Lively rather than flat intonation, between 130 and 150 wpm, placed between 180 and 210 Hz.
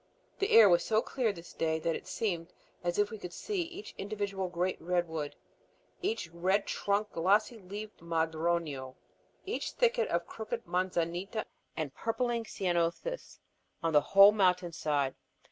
No: average, 4.4 semitones; average, 145 wpm; medium, 185 Hz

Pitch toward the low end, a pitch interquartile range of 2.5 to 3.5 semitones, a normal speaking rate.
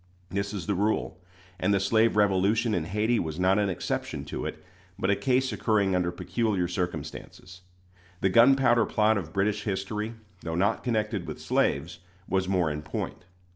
Yes: low, 100 Hz; average, 3.1 semitones; average, 170 wpm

